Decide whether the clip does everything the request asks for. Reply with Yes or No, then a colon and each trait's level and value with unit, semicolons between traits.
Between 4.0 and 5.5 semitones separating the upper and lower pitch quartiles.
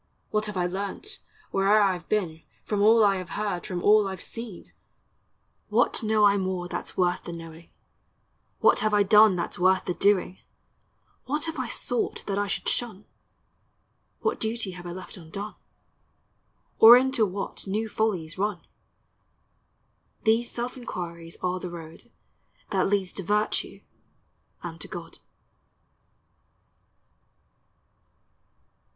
No: average, 3.1 semitones